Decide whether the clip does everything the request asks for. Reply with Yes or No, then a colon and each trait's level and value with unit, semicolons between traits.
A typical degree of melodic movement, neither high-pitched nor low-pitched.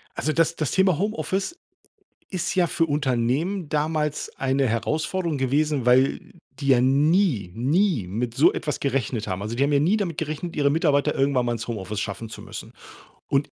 Yes: average, 4.9 semitones; medium, 145 Hz